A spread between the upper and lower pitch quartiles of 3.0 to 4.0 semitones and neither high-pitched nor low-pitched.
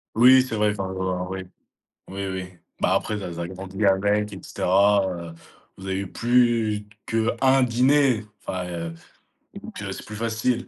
No: average, 3.5 semitones; low, 105 Hz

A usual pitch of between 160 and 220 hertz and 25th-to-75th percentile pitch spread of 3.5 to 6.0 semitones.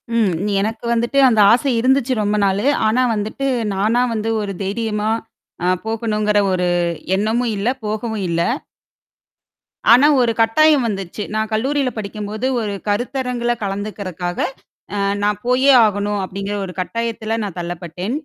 No: high, 215 Hz; average, 2.9 semitones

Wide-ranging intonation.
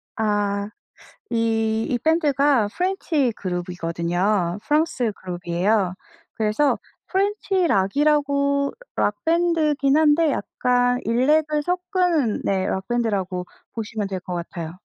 Yes: wide, 7.3 semitones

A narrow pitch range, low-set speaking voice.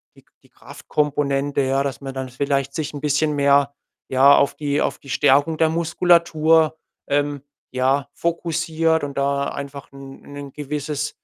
No: narrow, 2.2 semitones; medium, 145 Hz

